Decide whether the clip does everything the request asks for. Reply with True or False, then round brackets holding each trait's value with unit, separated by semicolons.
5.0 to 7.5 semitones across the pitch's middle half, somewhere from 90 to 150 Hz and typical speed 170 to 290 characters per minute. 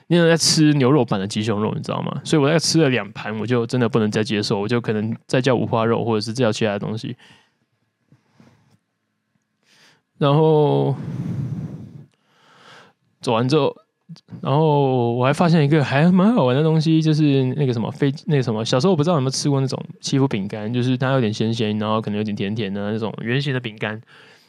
False (5.6 semitones; 135 Hz; 300 characters per minute)